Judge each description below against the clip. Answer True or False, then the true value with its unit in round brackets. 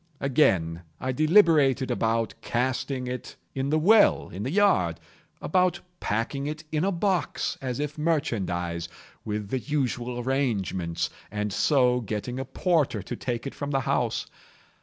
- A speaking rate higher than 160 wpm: False (140 wpm)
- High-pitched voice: False (130 Hz)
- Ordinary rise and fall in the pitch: False (6.0 semitones)